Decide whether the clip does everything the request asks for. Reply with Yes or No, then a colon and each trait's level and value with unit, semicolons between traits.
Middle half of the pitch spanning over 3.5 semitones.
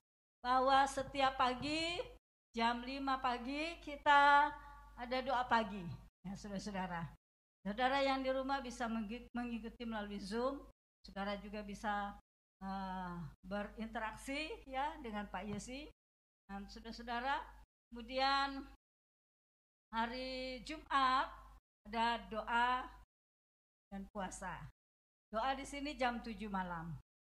Yes: average, 4.9 semitones